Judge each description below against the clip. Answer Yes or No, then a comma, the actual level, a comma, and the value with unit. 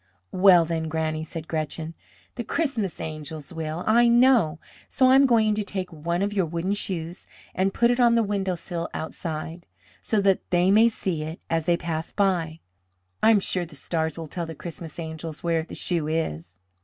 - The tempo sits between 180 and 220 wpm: Yes, average, 190 wpm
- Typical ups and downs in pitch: Yes, average, 3.9 semitones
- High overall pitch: No, medium, 170 Hz